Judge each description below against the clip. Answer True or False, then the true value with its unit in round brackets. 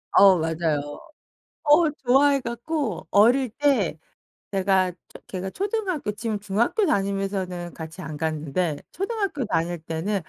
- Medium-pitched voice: False (200 Hz)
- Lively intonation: True (8.2 semitones)